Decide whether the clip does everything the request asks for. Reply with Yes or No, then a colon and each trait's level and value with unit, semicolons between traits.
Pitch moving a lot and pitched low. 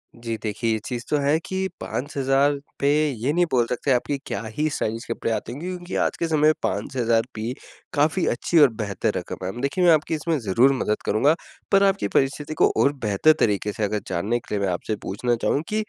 Yes: wide, 5.7 semitones; low, 130 Hz